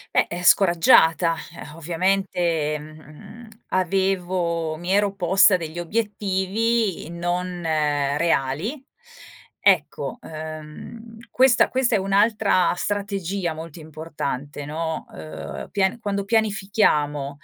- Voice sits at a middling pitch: Yes, medium, 175 Hz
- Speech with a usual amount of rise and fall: Yes, average, 4.1 semitones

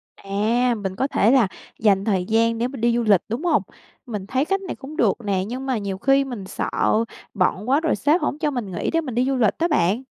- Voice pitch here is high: Yes, high, 235 Hz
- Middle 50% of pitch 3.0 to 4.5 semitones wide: No, average, 5.1 semitones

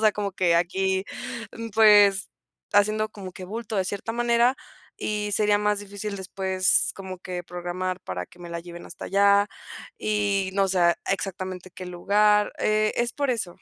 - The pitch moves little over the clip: Yes, narrow, 2.2 semitones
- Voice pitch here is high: Yes, high, 195 Hz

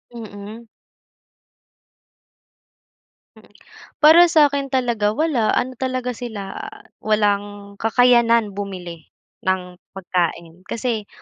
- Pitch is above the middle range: Yes, high, 220 Hz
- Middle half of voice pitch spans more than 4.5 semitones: No, average, 4.1 semitones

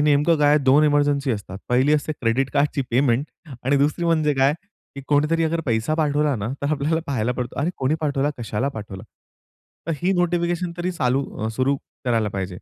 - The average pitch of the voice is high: No, medium, 140 Hz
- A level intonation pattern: No, average, 3.7 semitones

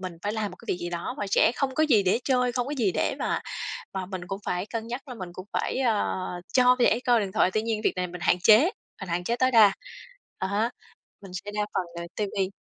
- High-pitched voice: Yes, high, 210 Hz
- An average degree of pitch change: Yes, average, 4.5 semitones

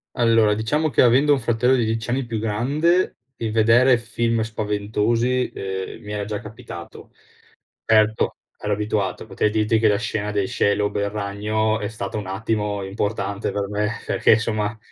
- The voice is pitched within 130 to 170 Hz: No, low, 110 Hz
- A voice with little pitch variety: Yes, narrow, 1.9 semitones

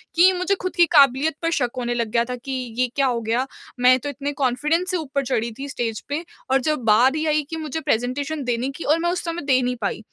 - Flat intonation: No, average, 4.2 semitones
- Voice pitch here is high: Yes, very high, 275 Hz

